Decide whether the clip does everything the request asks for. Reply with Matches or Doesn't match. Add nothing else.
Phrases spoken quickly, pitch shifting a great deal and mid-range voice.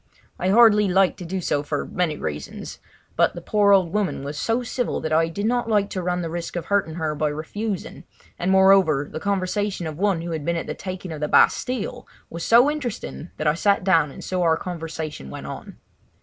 Doesn't match